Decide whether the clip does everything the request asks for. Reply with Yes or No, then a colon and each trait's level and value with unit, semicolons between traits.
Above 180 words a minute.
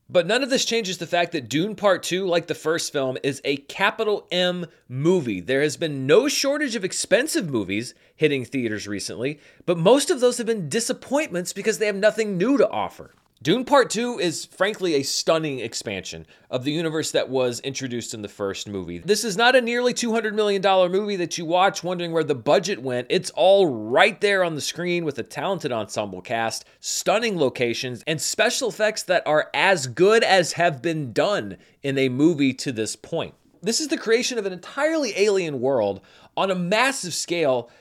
Yes: average, 195 wpm